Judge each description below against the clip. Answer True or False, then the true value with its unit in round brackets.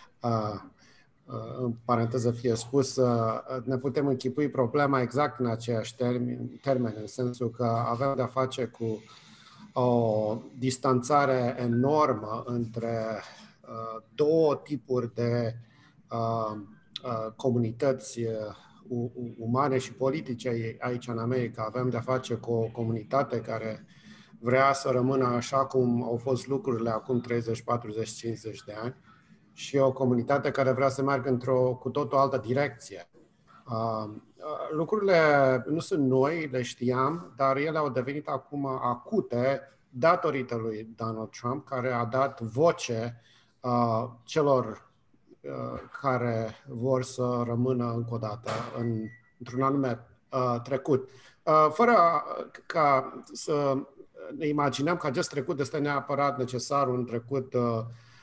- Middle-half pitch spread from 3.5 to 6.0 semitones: False (2.7 semitones)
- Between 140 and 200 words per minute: False (125 wpm)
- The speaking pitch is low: True (125 Hz)